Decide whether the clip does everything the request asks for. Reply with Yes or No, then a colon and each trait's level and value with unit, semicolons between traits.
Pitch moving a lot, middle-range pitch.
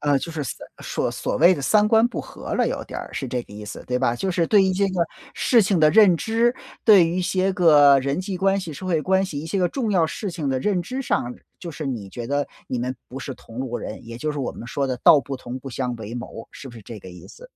Yes: wide, 6.9 semitones; medium, 155 Hz